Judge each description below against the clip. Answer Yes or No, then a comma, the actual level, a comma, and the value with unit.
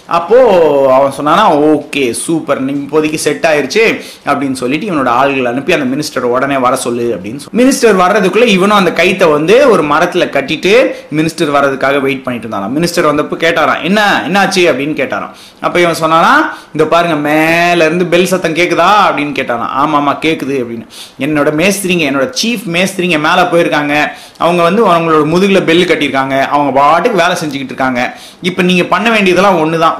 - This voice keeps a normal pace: No, fast, 160 wpm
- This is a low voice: No, medium, 160 Hz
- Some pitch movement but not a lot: Yes, average, 4.2 semitones